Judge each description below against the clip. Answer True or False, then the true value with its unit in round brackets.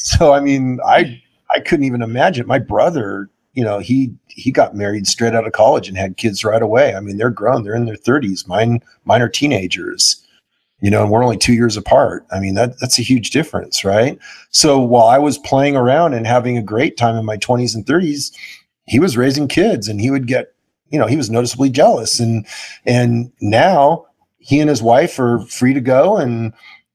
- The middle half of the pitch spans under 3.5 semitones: True (3.1 semitones)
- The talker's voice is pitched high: False (120 Hz)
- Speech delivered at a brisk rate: True (210 wpm)